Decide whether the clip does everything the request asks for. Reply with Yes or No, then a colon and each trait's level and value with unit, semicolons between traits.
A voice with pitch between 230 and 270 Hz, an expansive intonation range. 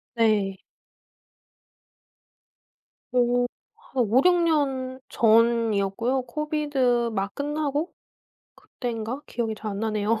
No: high, 240 Hz; average, 3.8 semitones